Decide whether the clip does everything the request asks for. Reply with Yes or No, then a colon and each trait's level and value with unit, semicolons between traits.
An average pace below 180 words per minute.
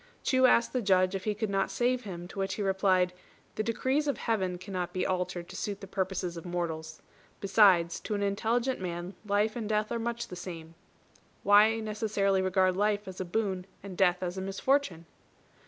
No: average, 195 wpm